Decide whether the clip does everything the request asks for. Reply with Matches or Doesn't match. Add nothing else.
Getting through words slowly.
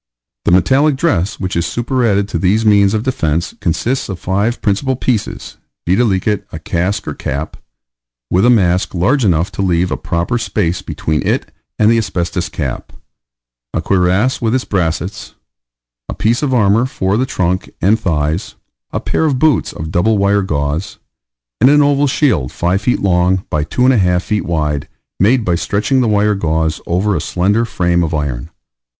Doesn't match